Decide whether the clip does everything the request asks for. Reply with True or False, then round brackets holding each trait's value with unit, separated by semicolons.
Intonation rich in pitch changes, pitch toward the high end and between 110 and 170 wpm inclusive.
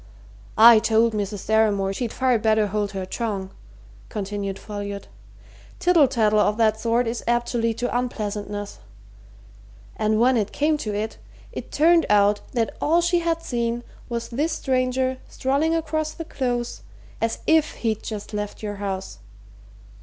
False (3.7 semitones; 230 Hz; 155 wpm)